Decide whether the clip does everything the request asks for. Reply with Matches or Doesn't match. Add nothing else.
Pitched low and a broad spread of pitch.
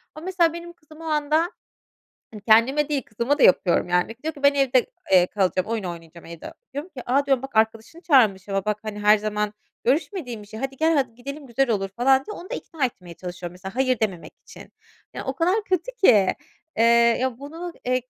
Doesn't match